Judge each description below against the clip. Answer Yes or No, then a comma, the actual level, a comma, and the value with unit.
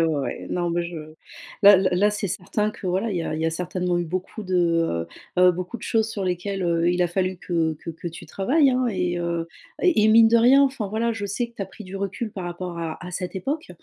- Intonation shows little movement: No, average, 3.7 semitones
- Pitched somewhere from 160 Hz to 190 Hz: Yes, medium, 185 Hz